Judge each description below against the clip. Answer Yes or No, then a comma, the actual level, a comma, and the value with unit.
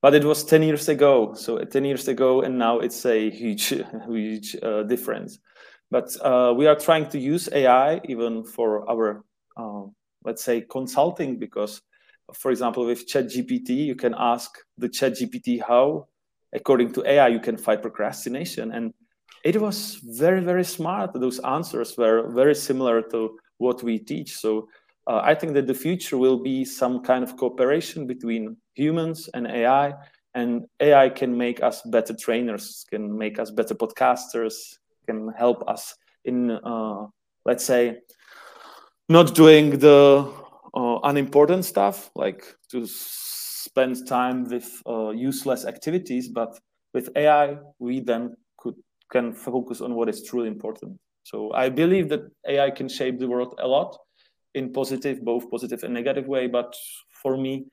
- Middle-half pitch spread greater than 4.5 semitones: No, average, 3.6 semitones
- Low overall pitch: Yes, low, 130 Hz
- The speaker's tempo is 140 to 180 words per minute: Yes, average, 160 wpm